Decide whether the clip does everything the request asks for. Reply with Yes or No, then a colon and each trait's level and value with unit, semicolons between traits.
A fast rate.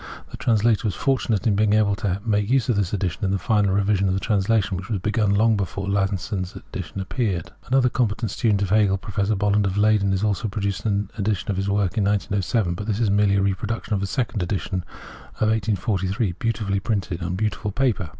Yes: fast, 210 wpm